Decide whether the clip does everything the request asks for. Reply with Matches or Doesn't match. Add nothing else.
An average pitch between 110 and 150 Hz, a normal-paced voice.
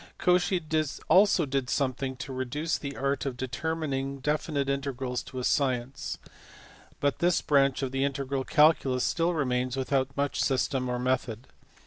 Matches